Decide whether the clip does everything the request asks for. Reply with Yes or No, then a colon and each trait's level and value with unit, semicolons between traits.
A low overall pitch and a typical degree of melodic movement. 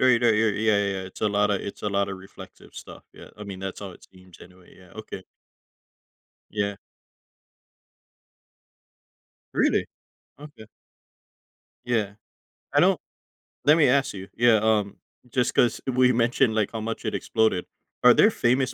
Yes: low, 110 Hz; average, 3.3 semitones